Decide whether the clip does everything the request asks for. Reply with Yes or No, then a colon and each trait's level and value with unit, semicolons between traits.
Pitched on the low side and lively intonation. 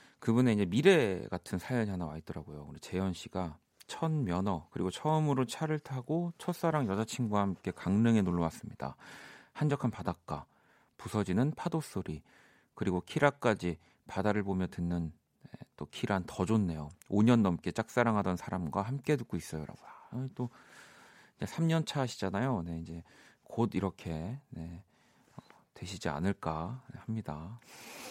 Yes: low, 105 Hz; wide, 6.5 semitones